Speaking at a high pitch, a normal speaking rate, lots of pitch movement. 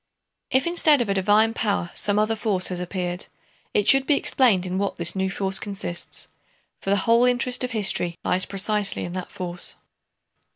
No: high, 200 Hz; average, 180 wpm; average, 3.6 semitones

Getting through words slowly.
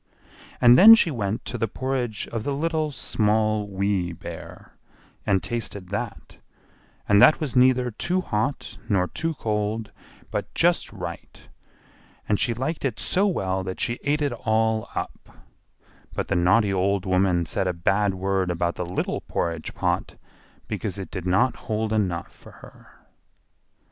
No: average, 155 wpm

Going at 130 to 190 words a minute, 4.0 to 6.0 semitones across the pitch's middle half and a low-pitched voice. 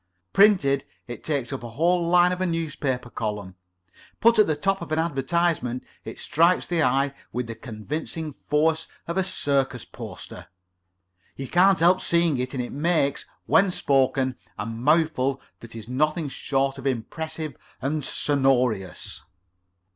No: average, 150 wpm; average, 4.7 semitones; medium, 145 Hz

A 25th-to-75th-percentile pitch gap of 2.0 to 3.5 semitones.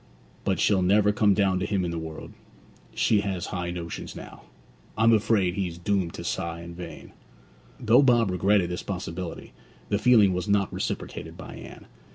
Yes: average, 2.9 semitones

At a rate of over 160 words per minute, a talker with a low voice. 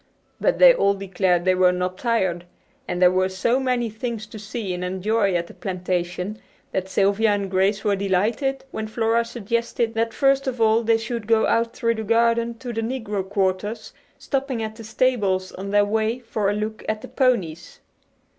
No: average, 190 wpm; high, 215 Hz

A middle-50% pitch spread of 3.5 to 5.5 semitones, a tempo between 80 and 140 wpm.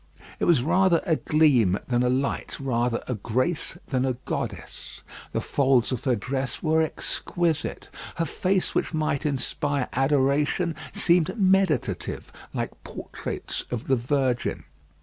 Yes: average, 4.2 semitones; slow, 135 wpm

